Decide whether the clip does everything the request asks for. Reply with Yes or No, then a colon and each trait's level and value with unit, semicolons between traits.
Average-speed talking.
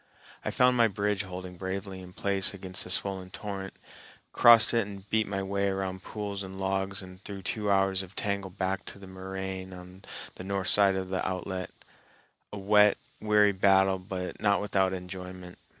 Yes: average, 175 wpm